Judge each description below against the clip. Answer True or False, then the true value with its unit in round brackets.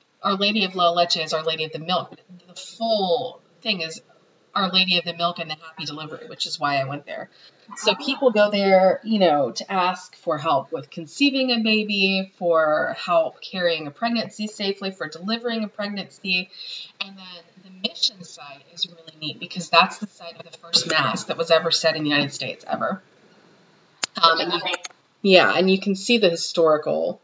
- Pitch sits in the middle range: True (180 Hz)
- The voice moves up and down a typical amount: True (3.5 semitones)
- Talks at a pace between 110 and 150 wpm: False (195 wpm)